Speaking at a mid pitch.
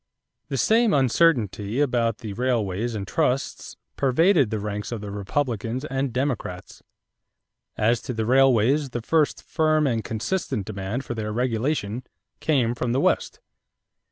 No: low, 120 Hz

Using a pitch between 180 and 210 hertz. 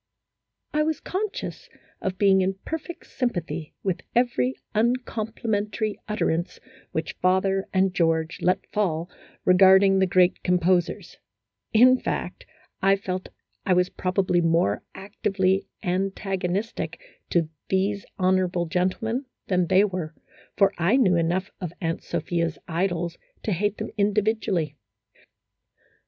Yes: high, 190 Hz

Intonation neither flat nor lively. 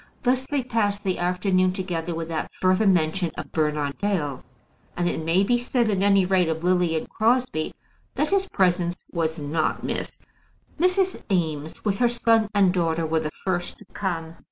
Yes: average, 4.5 semitones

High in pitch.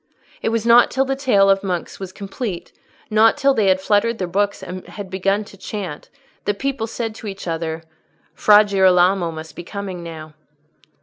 Yes: high, 195 Hz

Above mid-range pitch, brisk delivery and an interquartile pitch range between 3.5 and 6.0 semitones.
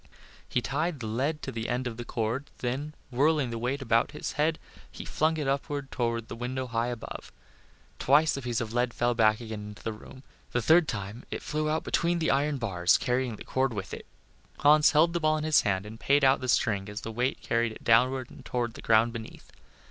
No: low, 125 Hz; fast, 225 wpm; average, 4.0 semitones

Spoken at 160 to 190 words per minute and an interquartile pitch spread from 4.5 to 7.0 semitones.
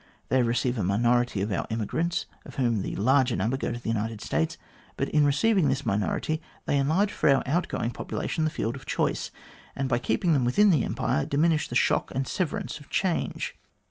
No: average, 200 wpm; average, 5.1 semitones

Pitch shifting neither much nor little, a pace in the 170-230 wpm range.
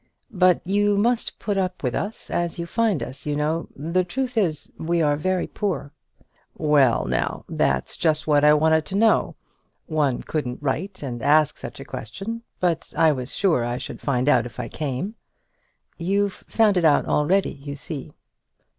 Yes: average, 4.9 semitones; average, 175 wpm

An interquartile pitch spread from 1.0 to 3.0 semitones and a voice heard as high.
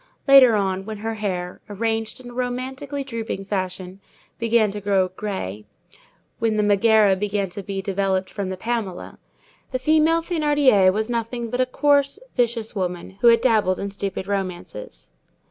No: average, 4.2 semitones; high, 215 Hz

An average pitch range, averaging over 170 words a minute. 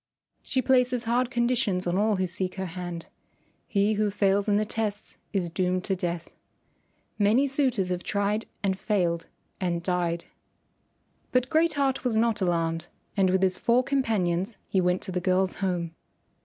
No: average, 4.1 semitones; average, 165 wpm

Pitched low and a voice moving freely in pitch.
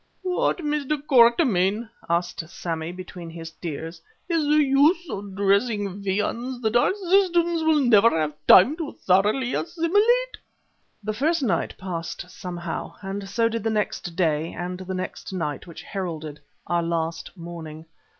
No: high, 200 Hz; wide, 8.3 semitones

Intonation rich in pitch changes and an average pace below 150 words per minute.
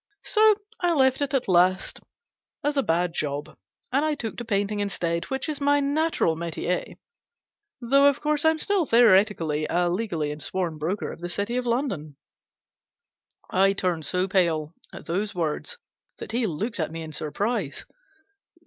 No: wide, 8.0 semitones; average, 160 wpm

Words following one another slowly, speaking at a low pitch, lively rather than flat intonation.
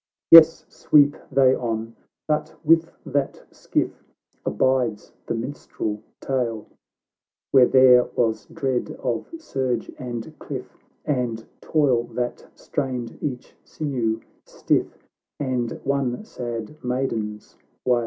No: slow, 110 wpm; low, 125 Hz; average, 2.9 semitones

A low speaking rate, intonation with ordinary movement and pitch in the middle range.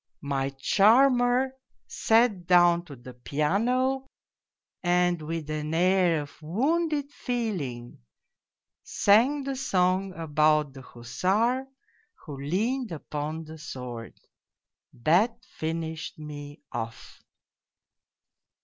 No: slow, 95 wpm; wide, 7.8 semitones; medium, 175 Hz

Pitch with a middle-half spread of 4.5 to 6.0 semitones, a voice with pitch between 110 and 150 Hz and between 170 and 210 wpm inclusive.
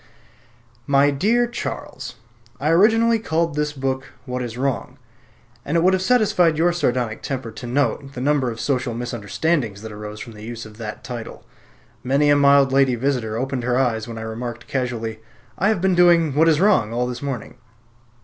Yes: average, 5.1 semitones; low, 135 Hz; average, 185 wpm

